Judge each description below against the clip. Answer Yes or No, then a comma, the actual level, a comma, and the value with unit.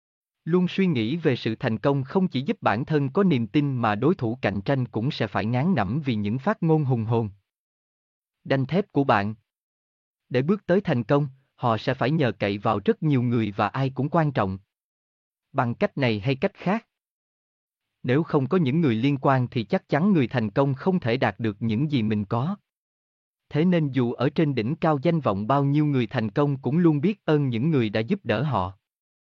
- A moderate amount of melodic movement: No, wide, 5.7 semitones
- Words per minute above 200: Yes, average, 215 wpm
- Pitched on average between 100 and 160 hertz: Yes, low, 135 Hz